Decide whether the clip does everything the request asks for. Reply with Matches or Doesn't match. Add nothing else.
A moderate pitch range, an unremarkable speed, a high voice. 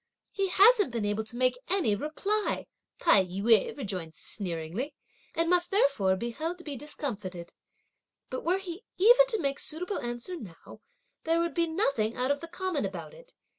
Doesn't match